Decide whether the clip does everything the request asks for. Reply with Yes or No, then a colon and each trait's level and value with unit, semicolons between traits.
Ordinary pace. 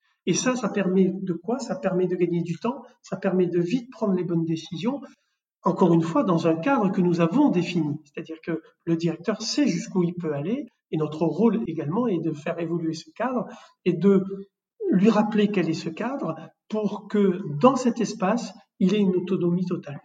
Yes: average, 200 wpm